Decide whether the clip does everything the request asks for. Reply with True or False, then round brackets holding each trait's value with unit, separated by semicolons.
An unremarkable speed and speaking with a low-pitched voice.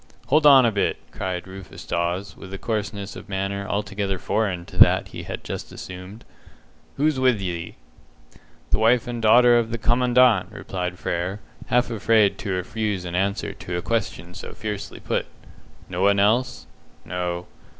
True (160 wpm; 100 Hz)